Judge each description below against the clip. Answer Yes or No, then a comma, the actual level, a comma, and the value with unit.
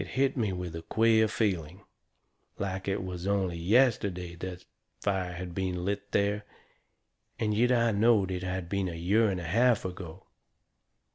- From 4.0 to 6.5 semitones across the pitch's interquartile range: No, average, 3.1 semitones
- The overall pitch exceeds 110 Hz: No, very low, 95 Hz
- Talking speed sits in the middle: Yes, average, 165 wpm